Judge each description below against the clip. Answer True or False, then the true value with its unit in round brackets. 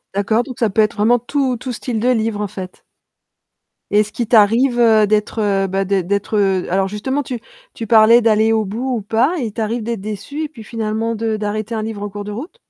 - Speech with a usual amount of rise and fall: False (2.3 semitones)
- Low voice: False (220 Hz)